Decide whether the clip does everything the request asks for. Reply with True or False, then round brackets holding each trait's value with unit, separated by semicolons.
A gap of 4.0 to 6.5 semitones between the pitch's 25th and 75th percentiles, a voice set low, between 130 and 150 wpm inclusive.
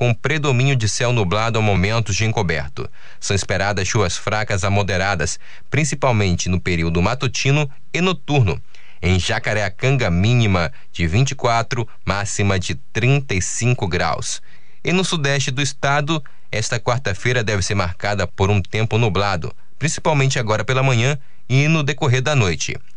True (5.5 semitones; 110 Hz; 140 wpm)